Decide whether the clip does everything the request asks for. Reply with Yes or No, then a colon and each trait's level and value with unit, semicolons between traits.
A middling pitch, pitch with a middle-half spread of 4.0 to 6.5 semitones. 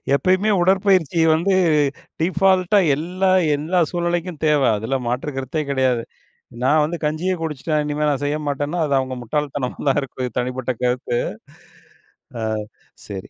Yes: medium, 150 Hz; average, 4.8 semitones